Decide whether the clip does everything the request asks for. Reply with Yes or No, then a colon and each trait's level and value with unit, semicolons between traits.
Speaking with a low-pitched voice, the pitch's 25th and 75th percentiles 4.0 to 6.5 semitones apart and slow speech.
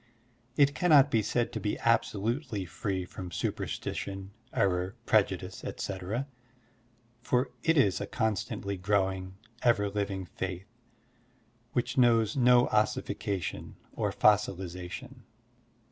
Yes: low, 105 Hz; average, 4.3 semitones; slow, 110 wpm